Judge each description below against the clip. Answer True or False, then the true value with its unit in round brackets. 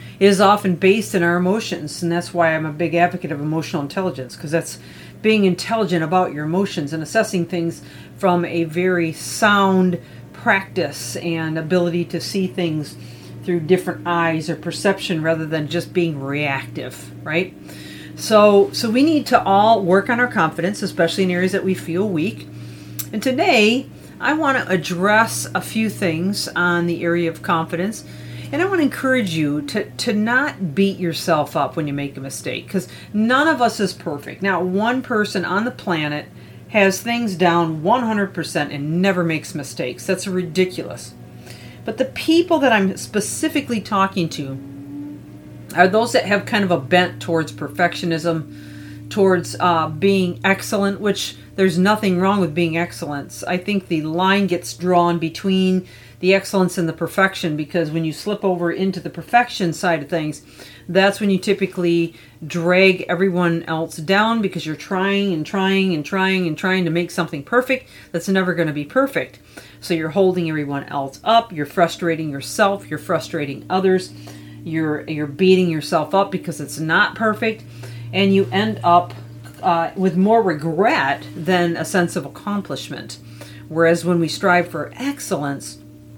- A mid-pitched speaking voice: True (175 Hz)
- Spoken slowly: False (165 wpm)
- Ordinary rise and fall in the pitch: True (3.5 semitones)